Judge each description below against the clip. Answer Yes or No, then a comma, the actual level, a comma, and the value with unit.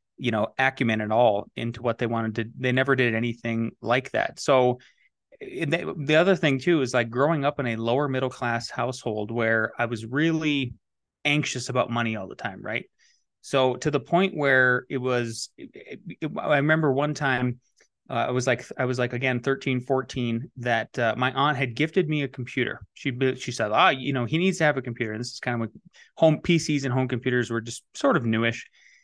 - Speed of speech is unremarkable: No, fast, 215 wpm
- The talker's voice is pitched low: Yes, low, 125 Hz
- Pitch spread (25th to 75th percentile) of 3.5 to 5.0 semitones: No, average, 3.0 semitones